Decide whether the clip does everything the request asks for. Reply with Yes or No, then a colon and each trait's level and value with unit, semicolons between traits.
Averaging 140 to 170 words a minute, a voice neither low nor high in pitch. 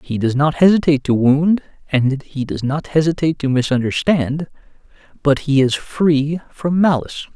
Yes: average, 155 wpm; medium, 145 Hz